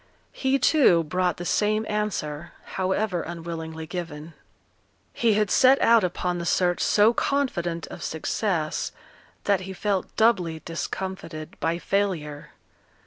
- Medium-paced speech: No, slow, 125 wpm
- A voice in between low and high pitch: Yes, medium, 180 Hz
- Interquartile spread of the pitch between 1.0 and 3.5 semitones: No, average, 4.1 semitones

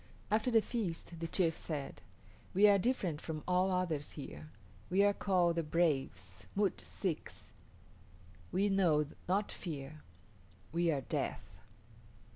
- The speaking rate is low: Yes, slow, 130 wpm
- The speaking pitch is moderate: Yes, medium, 170 Hz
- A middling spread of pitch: Yes, average, 4.5 semitones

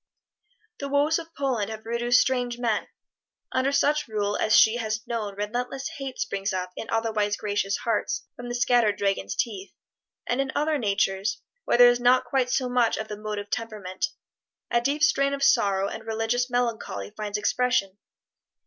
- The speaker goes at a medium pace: Yes, average, 170 wpm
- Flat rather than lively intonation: No, average, 3.3 semitones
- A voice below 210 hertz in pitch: No, high, 230 Hz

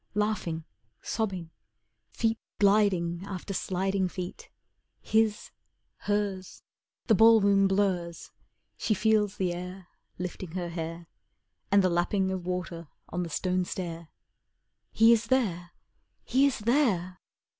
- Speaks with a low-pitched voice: No, high, 190 Hz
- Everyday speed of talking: No, slow, 115 wpm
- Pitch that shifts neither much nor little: Yes, average, 3.0 semitones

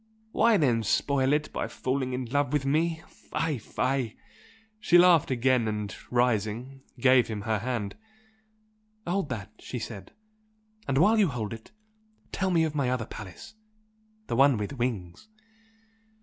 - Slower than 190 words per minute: Yes, average, 150 wpm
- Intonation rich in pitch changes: No, average, 4.6 semitones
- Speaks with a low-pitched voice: Yes, low, 130 Hz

